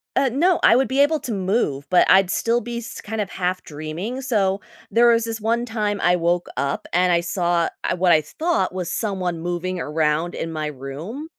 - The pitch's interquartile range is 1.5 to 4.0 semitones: No, average, 5.3 semitones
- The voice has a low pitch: No, medium, 185 Hz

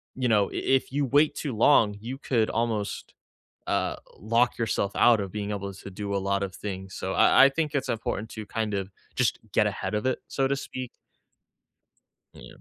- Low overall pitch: Yes, low, 110 Hz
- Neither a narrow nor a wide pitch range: Yes, average, 4.5 semitones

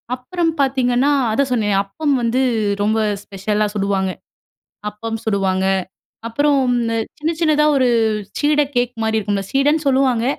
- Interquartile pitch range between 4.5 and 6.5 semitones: Yes, average, 4.9 semitones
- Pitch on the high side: Yes, high, 245 Hz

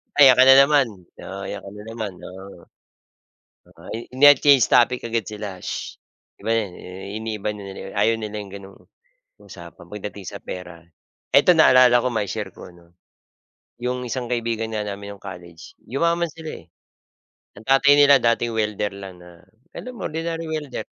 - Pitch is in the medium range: No, low, 110 Hz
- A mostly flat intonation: No, average, 4.7 semitones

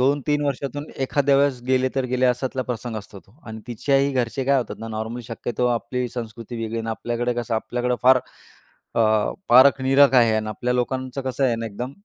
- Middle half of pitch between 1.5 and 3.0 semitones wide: Yes, narrow, 2.4 semitones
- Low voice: Yes, low, 125 Hz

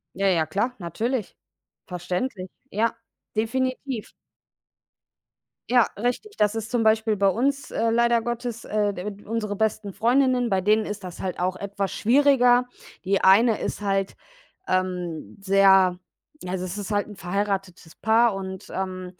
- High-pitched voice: Yes, high, 205 Hz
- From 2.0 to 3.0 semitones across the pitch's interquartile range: No, average, 3.6 semitones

